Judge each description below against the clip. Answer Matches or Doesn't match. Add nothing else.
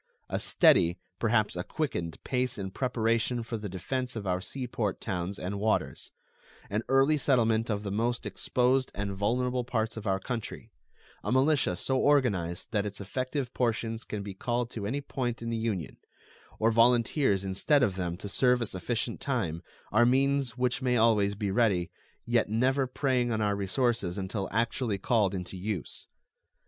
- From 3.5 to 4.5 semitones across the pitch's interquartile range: Matches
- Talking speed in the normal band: Matches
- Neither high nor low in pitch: Doesn't match